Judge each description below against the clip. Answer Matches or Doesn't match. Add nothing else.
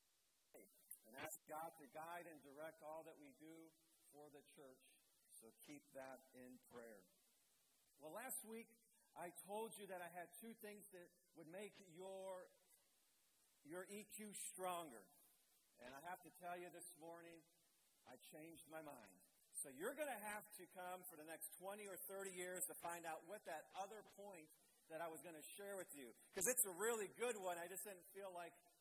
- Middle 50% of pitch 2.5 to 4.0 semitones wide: Matches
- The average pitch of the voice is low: Doesn't match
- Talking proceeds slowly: Doesn't match